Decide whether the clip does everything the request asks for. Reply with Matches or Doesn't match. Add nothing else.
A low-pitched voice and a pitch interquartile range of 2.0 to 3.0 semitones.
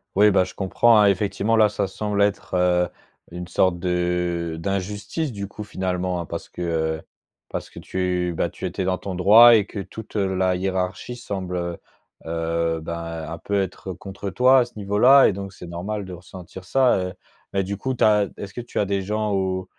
Matches